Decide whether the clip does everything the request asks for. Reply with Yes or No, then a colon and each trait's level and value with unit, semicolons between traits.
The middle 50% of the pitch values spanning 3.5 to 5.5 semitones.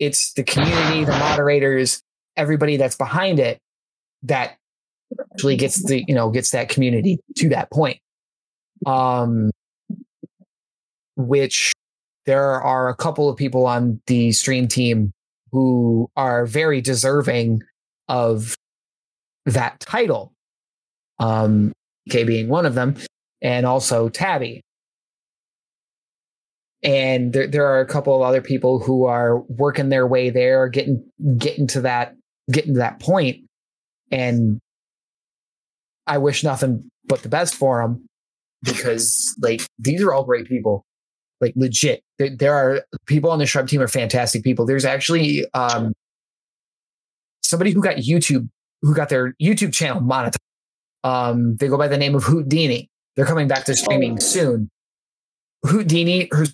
No: average, 3.0 semitones